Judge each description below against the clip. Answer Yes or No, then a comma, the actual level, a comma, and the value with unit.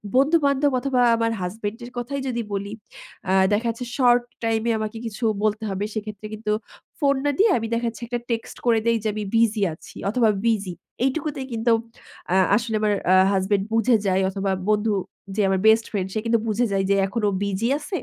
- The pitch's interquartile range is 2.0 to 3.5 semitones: Yes, average, 2.8 semitones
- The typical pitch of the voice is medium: No, high, 225 Hz